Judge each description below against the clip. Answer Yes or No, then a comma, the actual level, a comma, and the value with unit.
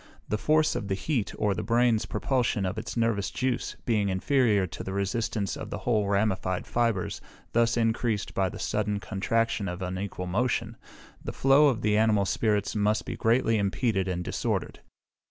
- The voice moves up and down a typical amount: Yes, average, 3.0 semitones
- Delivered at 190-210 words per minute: No, average, 170 wpm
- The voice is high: No, low, 105 Hz